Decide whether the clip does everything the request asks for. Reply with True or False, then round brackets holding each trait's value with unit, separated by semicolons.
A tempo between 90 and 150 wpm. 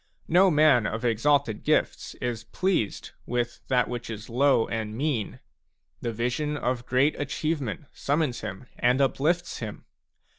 True (145 wpm)